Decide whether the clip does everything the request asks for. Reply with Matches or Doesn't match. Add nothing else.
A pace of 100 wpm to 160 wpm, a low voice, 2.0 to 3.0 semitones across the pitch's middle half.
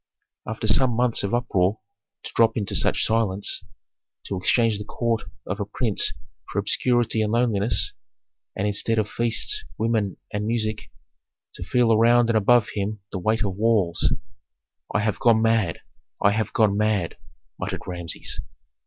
Matches